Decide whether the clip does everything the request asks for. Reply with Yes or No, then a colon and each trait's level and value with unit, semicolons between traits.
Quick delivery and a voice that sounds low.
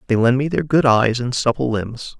Yes: fast, 245 wpm; low, 125 Hz